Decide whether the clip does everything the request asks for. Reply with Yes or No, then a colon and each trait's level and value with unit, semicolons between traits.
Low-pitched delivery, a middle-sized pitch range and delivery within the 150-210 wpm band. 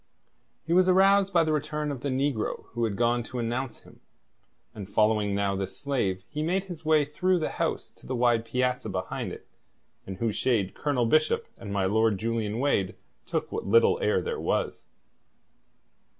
No: low, 120 Hz; wide, 6.1 semitones; average, 180 wpm